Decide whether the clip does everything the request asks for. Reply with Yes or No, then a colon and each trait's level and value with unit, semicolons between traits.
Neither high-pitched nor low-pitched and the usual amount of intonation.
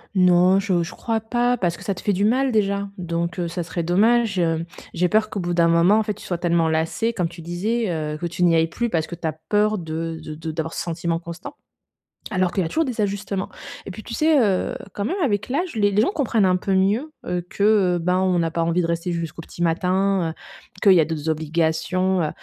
Yes: medium, 180 Hz; average, 3.8 semitones